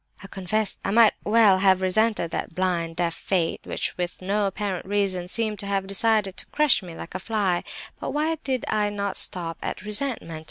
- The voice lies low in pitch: No, high, 195 Hz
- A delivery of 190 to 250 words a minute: Yes, average, 195 wpm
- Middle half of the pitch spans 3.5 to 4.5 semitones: No, average, 2.9 semitones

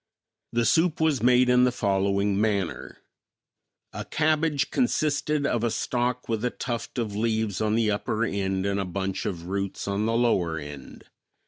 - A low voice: Yes, low, 110 Hz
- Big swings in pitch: No, average, 4.1 semitones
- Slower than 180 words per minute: Yes, average, 165 wpm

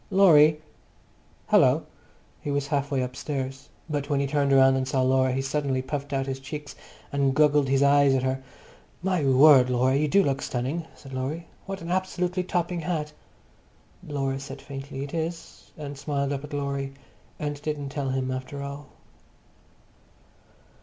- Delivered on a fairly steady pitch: Yes, narrow, 2.1 semitones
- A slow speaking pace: No, average, 165 wpm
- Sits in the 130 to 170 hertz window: Yes, medium, 140 Hz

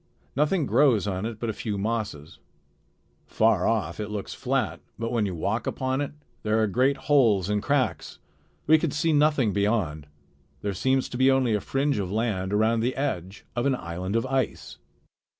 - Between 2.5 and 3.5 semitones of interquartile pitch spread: No, average, 4.8 semitones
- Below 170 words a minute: No, average, 185 wpm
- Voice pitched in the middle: No, low, 115 Hz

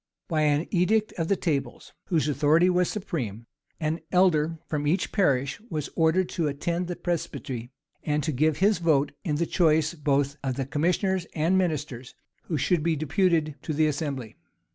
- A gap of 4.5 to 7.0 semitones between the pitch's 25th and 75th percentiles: No, average, 3.3 semitones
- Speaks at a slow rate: No, average, 170 wpm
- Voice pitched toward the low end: No, medium, 155 Hz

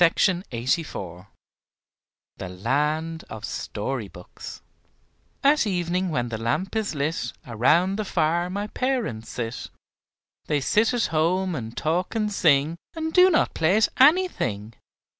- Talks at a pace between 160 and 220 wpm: No, slow, 135 wpm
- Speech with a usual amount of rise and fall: No, wide, 8.9 semitones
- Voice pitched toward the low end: No, medium, 165 Hz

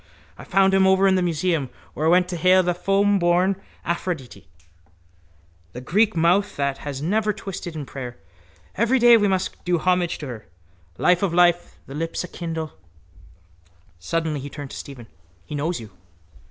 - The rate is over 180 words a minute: No, average, 170 wpm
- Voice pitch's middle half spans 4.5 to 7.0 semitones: No, average, 4.1 semitones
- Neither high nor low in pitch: Yes, medium, 175 Hz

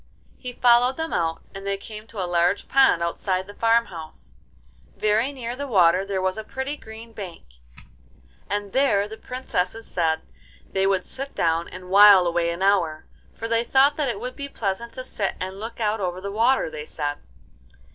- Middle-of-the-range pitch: No, high, 205 Hz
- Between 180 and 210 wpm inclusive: Yes, average, 190 wpm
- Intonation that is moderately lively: Yes, average, 4.4 semitones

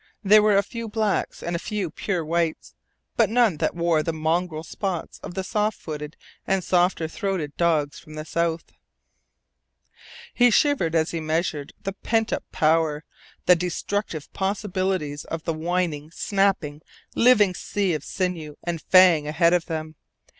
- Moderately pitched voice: Yes, medium, 170 Hz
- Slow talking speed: No, average, 155 wpm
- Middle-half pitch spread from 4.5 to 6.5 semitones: No, average, 3.7 semitones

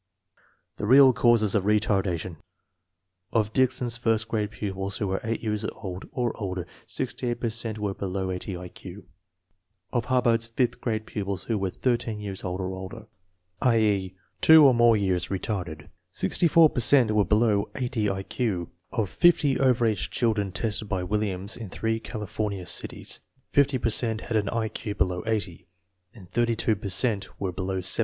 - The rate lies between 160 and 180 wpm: Yes, average, 170 wpm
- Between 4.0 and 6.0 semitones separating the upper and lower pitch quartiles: No, average, 3.4 semitones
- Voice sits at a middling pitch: No, low, 105 Hz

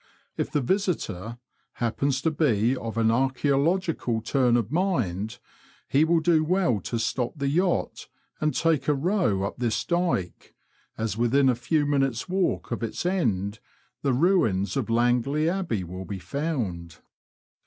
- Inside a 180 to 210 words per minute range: No, average, 150 wpm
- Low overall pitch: Yes, low, 130 Hz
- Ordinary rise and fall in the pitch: No, wide, 6.0 semitones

